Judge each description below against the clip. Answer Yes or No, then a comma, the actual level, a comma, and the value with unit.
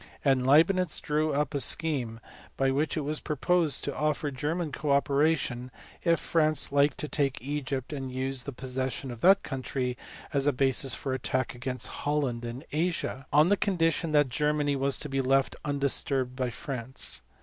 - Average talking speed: Yes, average, 170 wpm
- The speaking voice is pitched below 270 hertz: Yes, medium, 140 Hz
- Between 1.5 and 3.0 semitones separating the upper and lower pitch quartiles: Yes, narrow, 2.6 semitones